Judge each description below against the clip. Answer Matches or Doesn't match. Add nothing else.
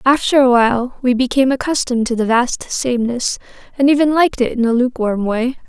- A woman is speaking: Matches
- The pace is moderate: Matches